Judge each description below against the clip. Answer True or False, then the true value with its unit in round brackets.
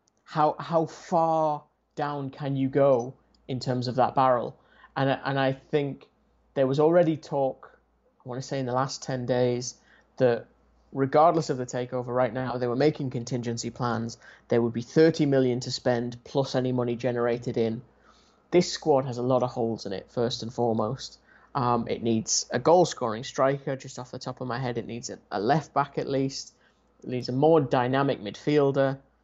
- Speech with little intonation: True (2.3 semitones)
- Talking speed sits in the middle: True (190 wpm)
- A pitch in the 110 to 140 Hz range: True (130 Hz)